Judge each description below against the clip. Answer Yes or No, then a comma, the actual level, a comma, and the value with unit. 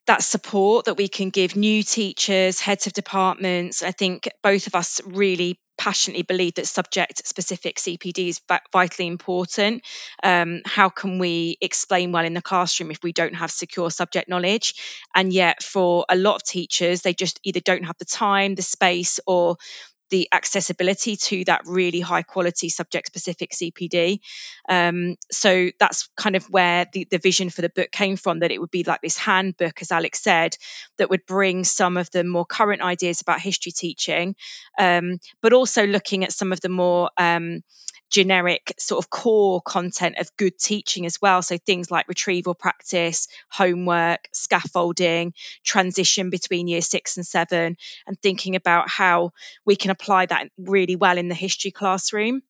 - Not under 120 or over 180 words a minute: Yes, average, 175 wpm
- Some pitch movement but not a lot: No, narrow, 1.8 semitones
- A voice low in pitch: No, medium, 180 Hz